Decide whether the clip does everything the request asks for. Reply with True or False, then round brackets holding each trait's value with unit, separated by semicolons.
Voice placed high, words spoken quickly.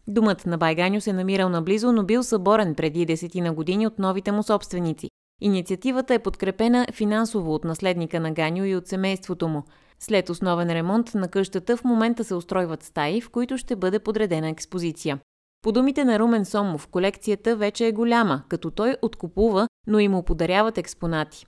True (195 Hz; 170 wpm)